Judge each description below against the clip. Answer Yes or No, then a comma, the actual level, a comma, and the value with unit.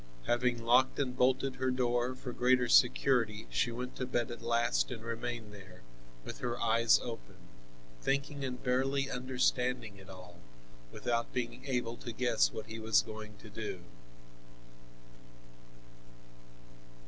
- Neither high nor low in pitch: No, low, 120 Hz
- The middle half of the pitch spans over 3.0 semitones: No, narrow, 2.4 semitones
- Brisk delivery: No, slow, 135 wpm